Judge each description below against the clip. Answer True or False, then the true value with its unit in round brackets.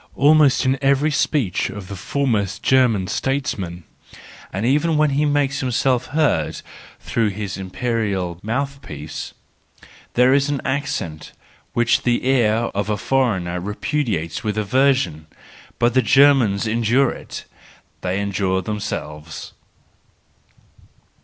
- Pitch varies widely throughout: True (5.8 semitones)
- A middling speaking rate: False (115 wpm)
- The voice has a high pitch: False (120 Hz)